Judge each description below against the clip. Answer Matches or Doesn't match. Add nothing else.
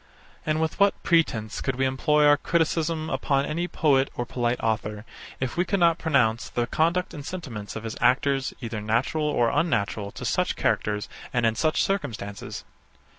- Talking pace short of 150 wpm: Doesn't match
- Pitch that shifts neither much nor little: Doesn't match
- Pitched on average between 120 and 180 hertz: Matches